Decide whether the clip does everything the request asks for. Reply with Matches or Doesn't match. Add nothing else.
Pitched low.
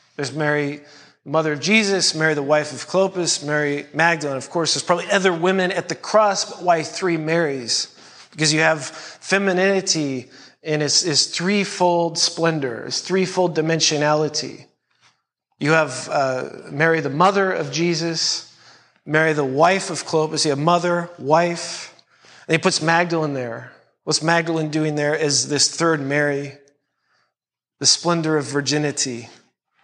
Doesn't match